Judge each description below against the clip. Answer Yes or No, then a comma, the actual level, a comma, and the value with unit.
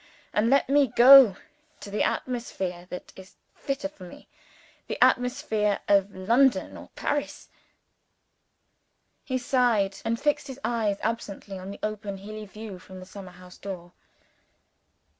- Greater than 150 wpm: No, average, 140 wpm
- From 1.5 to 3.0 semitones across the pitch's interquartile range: No, average, 4.4 semitones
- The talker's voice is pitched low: No, high, 210 Hz